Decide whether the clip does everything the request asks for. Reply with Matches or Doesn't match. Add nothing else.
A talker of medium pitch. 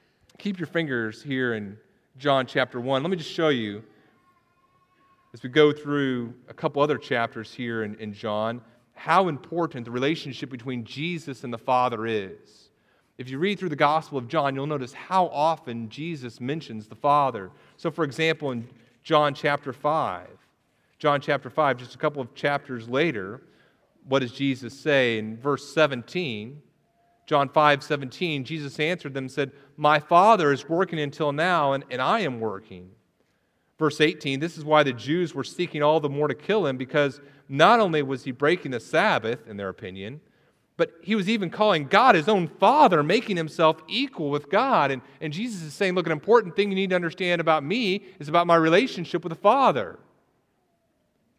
Matches